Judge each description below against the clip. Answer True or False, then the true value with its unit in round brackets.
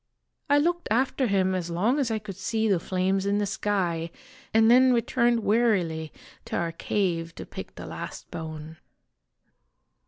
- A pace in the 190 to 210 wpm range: False (160 wpm)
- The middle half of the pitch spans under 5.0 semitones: False (5.3 semitones)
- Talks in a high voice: True (200 Hz)